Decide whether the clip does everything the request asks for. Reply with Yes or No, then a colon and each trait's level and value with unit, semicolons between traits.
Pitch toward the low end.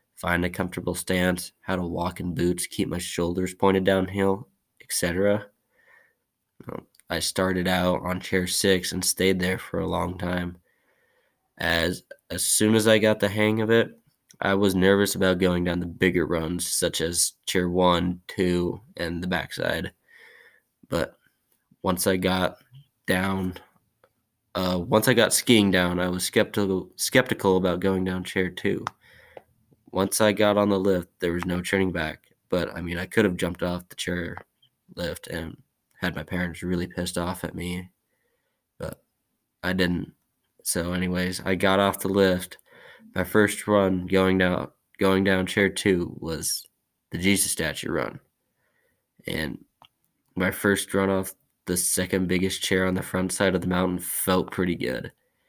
Yes: very low, 90 Hz